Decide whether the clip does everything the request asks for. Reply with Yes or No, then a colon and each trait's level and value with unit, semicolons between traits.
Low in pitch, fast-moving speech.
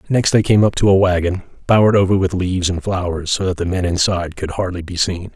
Yes: very low, 90 Hz; fast, 245 wpm